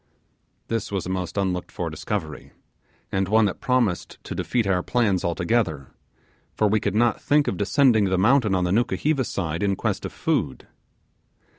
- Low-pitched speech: Yes, low, 100 Hz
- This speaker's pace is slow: No, average, 170 wpm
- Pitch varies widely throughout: No, average, 4.2 semitones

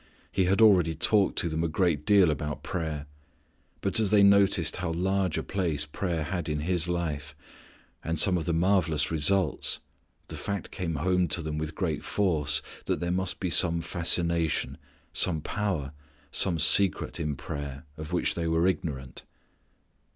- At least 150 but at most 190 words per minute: Yes, average, 165 wpm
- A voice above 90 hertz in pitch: No, very low, 85 Hz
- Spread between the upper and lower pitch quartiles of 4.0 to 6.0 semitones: No, average, 3.3 semitones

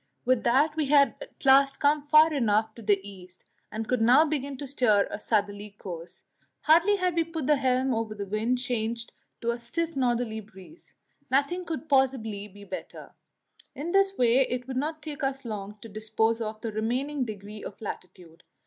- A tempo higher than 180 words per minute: Yes, average, 190 wpm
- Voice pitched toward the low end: No, high, 245 Hz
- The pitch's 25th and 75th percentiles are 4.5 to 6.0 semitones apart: Yes, average, 5.0 semitones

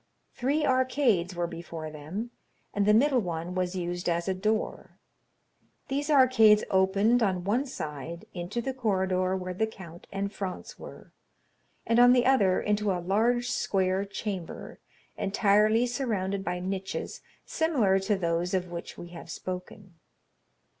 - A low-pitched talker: No, high, 195 Hz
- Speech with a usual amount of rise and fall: Yes, average, 4.2 semitones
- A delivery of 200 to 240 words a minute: No, average, 145 wpm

